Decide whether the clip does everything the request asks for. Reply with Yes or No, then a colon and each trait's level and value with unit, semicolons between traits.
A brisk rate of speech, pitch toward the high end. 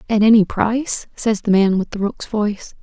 Yes: fast, 215 wpm; high, 210 Hz